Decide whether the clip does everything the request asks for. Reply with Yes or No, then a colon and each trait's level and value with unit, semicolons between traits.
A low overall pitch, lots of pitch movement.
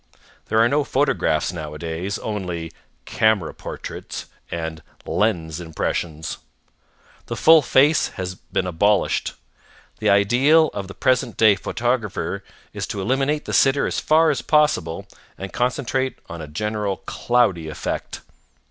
Yes: low, 105 Hz; wide, 7.5 semitones